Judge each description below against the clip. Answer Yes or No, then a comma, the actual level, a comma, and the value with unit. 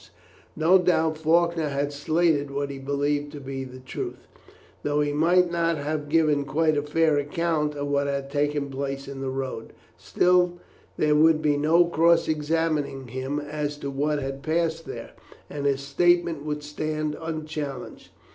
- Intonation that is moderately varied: No, narrow, 2.3 semitones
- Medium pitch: Yes, medium, 150 Hz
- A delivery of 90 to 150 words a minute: No, average, 165 wpm